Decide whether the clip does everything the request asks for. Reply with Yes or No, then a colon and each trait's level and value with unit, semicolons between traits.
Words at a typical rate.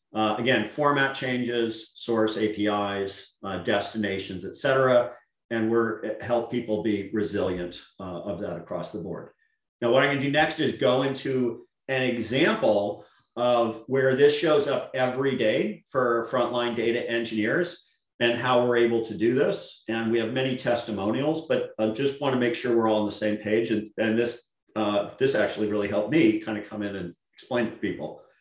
Yes: average, 185 wpm